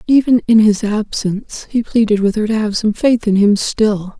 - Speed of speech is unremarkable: No, fast, 215 wpm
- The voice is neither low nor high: No, high, 215 Hz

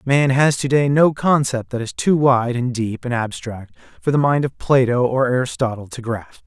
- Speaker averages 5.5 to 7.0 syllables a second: No, 4.8 syllables/s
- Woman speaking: No, male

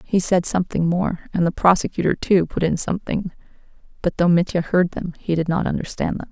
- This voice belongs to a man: No, female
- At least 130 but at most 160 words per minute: No, average, 200 wpm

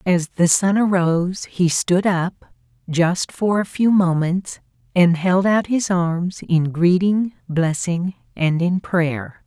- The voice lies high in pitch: No, medium, 180 Hz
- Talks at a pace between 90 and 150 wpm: Yes, average, 145 wpm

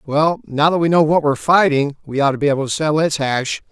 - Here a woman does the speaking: No, male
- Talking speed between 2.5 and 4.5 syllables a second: No, 6.5 syllables/s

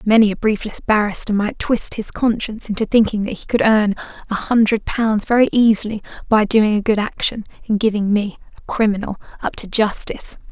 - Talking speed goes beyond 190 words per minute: No, average, 175 wpm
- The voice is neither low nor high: No, high, 215 Hz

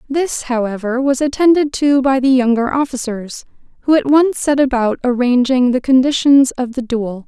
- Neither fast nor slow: Yes, average, 165 wpm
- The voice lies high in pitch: Yes, very high, 260 Hz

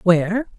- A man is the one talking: No, female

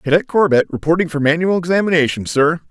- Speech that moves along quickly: No, average, 155 wpm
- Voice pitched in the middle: Yes, medium, 165 Hz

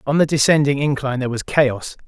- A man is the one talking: Yes, male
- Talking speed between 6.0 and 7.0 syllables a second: Yes, 6.4 syllables/s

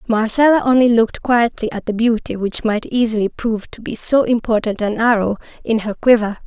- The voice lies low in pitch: No, high, 225 Hz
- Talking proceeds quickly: No, average, 185 wpm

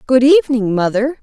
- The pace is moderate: Yes, average, 145 wpm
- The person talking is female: Yes, female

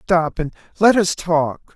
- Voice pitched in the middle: Yes, medium, 175 Hz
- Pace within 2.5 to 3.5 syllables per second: Yes, 3.4 syllables/s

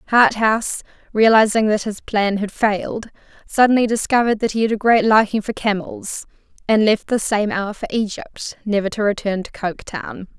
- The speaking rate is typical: Yes, average, 165 wpm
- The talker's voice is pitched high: Yes, high, 215 Hz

